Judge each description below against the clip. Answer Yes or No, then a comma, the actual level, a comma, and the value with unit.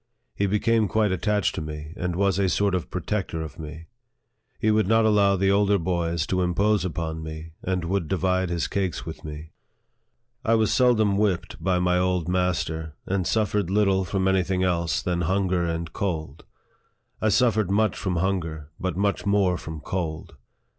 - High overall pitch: No, very low, 95 Hz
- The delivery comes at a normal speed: Yes, average, 180 wpm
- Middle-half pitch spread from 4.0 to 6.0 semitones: No, average, 3.2 semitones